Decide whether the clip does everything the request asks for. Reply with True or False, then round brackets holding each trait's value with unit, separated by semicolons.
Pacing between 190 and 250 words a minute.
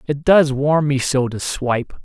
True (205 wpm)